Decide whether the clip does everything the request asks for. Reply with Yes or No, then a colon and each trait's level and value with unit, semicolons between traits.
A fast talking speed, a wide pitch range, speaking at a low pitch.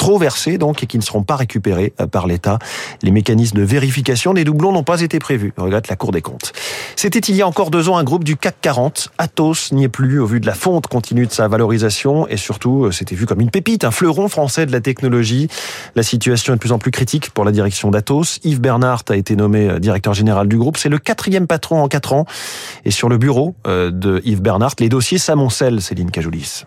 Yes: fast, 235 wpm; wide, 6.2 semitones; low, 125 Hz